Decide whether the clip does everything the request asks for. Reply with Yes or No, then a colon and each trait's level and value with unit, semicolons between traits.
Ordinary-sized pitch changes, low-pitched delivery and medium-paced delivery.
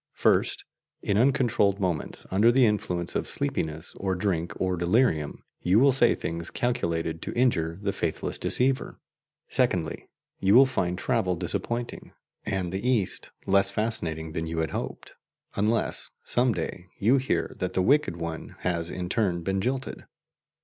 No: wide, 5.7 semitones; very low, 95 Hz; average, 150 wpm